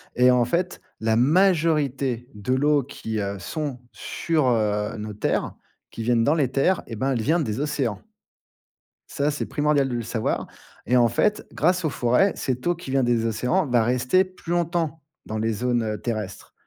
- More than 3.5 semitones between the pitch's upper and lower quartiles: Yes, average, 5.1 semitones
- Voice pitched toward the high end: No, low, 125 Hz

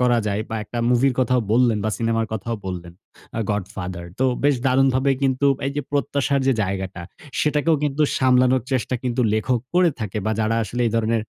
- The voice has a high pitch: No, low, 120 Hz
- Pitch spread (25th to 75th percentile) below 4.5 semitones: Yes, average, 3.6 semitones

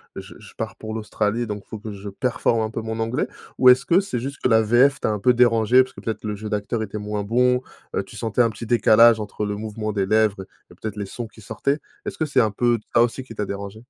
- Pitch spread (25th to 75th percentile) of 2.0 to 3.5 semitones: Yes, narrow, 2.5 semitones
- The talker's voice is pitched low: Yes, low, 110 Hz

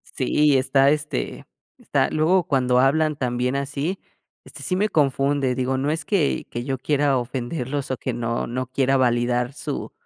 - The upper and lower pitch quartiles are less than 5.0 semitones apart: Yes, average, 2.9 semitones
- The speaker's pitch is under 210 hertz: Yes, low, 135 Hz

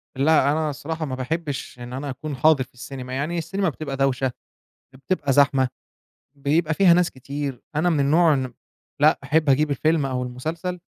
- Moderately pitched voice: Yes, medium, 145 Hz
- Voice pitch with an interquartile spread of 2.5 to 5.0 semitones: Yes, average, 3.2 semitones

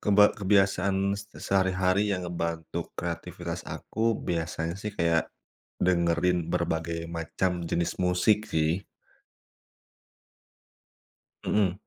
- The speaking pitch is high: No, very low, 90 Hz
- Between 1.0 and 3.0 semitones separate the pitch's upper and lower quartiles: Yes, narrow, 2.6 semitones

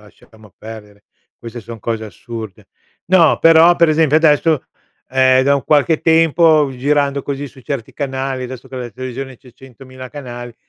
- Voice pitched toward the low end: Yes, low, 130 Hz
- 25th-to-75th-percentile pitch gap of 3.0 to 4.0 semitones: Yes, average, 3.6 semitones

